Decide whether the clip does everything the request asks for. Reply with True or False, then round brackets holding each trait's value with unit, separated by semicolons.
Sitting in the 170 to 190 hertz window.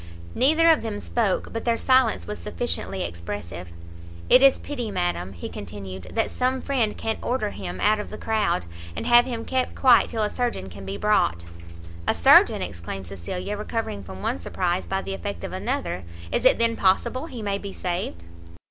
False (205 Hz)